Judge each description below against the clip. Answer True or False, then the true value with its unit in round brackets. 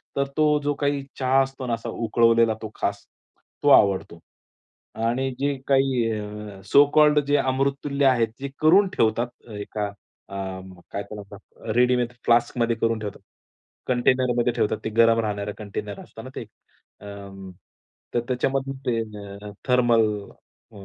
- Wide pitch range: False (3.8 semitones)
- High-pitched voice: False (120 Hz)